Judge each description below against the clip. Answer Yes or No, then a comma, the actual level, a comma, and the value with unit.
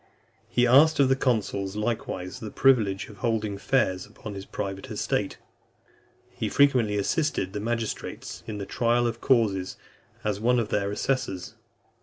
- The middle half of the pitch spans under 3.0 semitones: No, average, 3.7 semitones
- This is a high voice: No, low, 110 Hz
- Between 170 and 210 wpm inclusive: No, average, 150 wpm